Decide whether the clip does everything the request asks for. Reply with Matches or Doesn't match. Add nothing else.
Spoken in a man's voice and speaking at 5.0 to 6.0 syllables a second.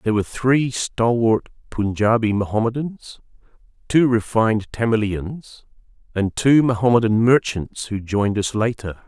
Doesn't match